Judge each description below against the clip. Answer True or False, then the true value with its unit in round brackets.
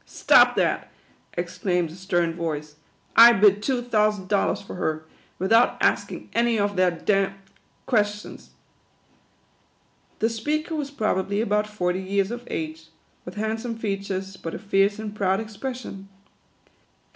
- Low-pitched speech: False (200 Hz)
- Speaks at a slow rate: False (155 wpm)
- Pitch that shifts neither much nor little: True (3.1 semitones)